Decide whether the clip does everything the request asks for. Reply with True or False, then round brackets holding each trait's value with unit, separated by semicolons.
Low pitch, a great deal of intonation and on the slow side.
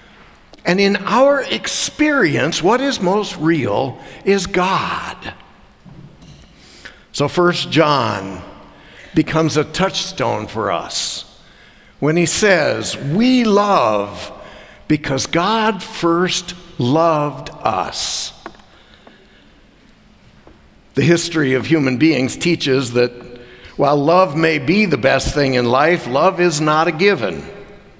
False (165 Hz; 5.7 semitones; 105 wpm)